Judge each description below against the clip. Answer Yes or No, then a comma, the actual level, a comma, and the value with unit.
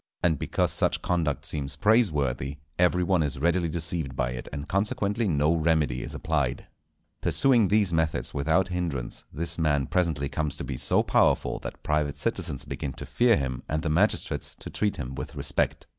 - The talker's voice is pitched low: Yes, very low, 80 Hz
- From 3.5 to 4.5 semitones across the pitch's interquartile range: Yes, average, 4.1 semitones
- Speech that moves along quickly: No, average, 175 wpm